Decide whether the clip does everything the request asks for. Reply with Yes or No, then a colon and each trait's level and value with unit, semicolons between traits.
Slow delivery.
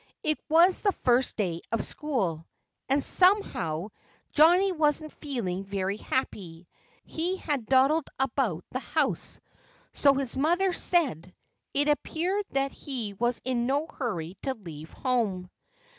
Yes: slow, 130 wpm